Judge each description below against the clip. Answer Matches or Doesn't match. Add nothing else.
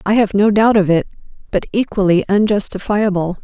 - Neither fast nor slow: Matches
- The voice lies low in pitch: Doesn't match